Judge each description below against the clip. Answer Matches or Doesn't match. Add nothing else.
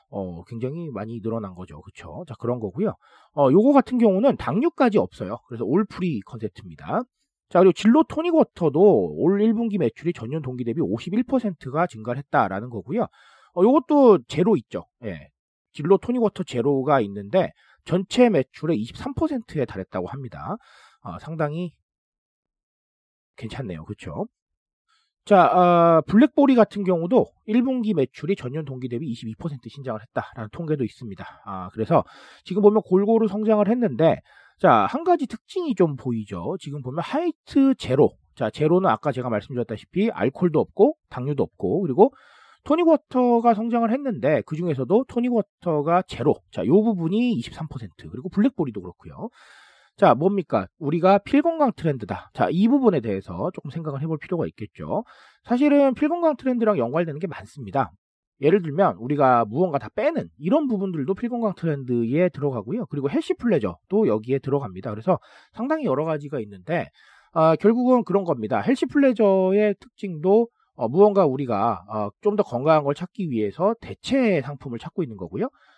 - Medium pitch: Matches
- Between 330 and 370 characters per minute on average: Matches